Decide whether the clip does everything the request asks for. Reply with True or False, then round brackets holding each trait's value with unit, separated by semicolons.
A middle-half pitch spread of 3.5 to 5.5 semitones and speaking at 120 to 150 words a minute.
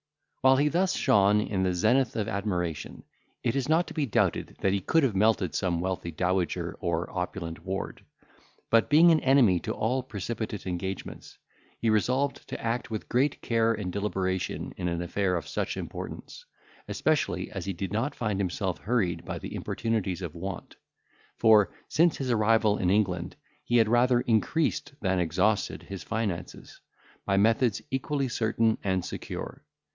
False (4.4 semitones; 165 wpm)